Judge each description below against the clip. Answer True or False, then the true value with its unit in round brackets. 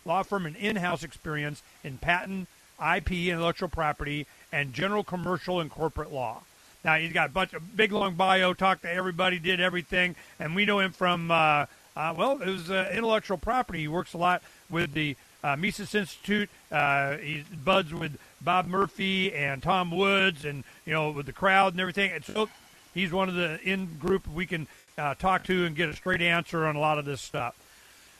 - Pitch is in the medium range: True (180 Hz)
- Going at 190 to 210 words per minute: True (200 wpm)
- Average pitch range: True (3.5 semitones)